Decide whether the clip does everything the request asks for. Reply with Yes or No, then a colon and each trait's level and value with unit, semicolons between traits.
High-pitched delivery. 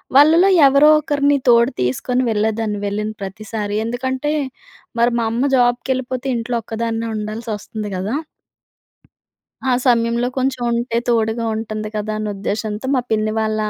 Yes: high, 230 Hz